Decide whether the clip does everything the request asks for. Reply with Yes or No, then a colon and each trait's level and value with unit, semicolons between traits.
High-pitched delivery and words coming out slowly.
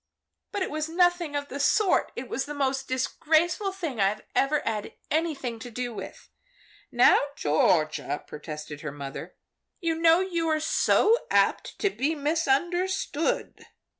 No: very high, 295 Hz; average, 145 wpm